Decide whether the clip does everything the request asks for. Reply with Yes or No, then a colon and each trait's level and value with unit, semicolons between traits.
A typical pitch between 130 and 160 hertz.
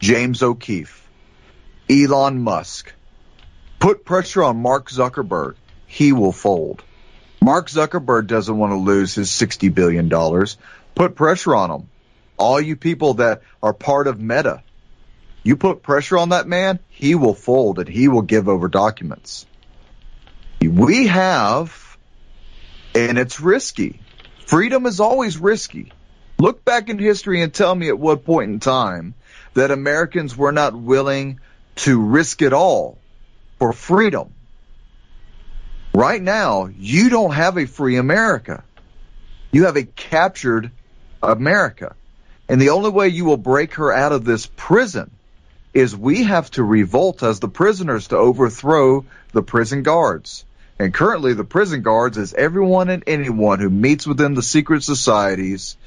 Yes: low, 135 Hz